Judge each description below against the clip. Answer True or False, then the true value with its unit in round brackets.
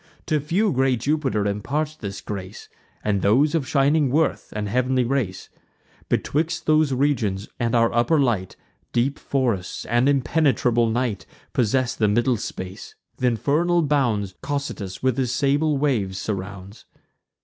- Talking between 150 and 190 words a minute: False (140 wpm)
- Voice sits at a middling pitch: False (125 Hz)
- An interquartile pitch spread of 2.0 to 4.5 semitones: False (5.3 semitones)